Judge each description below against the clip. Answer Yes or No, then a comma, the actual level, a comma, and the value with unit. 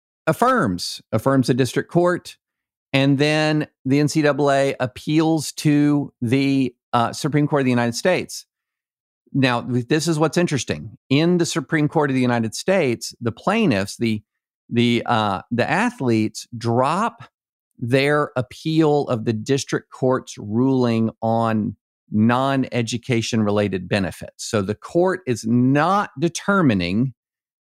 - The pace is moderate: No, slow, 125 wpm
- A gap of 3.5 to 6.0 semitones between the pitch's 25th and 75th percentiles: Yes, average, 4.2 semitones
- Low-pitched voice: Yes, low, 130 Hz